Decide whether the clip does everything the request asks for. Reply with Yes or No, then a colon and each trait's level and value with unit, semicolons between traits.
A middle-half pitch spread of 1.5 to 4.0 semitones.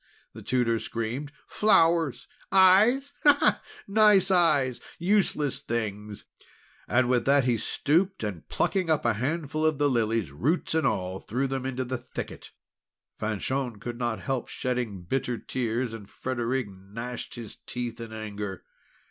No: wide, 5.4 semitones